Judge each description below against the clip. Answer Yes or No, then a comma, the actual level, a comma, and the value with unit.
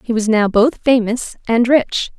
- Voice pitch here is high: Yes, high, 235 Hz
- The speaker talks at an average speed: Yes, average, 190 wpm